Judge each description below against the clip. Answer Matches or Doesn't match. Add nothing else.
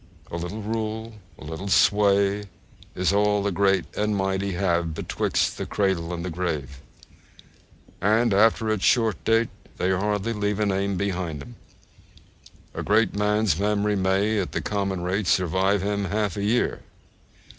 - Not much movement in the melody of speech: Matches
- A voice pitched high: Doesn't match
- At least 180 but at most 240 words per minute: Doesn't match